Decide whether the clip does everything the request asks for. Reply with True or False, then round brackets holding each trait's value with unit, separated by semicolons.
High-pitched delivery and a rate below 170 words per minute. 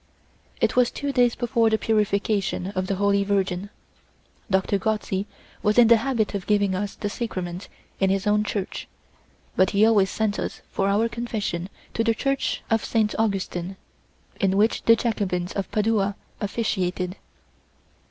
True (205 Hz; 155 wpm)